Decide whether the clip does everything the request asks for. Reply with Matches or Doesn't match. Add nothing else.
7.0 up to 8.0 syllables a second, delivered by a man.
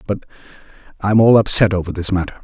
Matches